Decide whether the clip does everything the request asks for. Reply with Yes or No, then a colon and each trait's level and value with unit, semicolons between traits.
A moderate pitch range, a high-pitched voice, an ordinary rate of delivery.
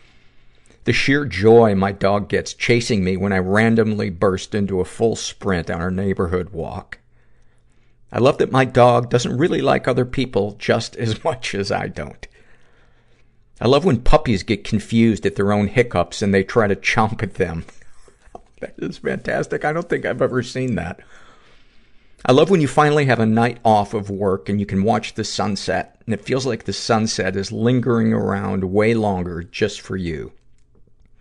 No: average, 3.3 semitones; low, 105 Hz; average, 180 wpm